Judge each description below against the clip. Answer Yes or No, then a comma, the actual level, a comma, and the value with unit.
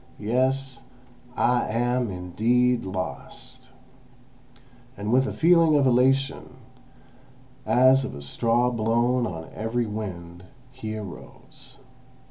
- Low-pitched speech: Yes, low, 120 Hz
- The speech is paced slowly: Yes, slow, 100 wpm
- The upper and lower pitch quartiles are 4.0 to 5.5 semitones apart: No, average, 3.6 semitones